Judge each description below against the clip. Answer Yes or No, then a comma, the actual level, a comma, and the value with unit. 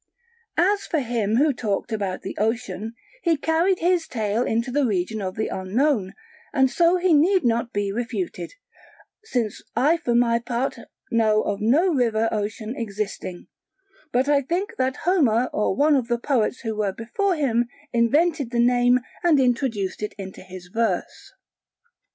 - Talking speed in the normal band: Yes, average, 160 wpm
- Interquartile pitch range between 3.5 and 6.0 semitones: Yes, average, 5.3 semitones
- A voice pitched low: No, high, 240 Hz